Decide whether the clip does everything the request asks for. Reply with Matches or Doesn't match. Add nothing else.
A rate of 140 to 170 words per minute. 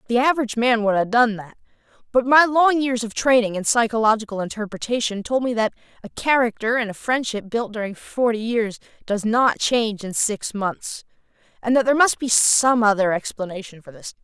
Doesn't match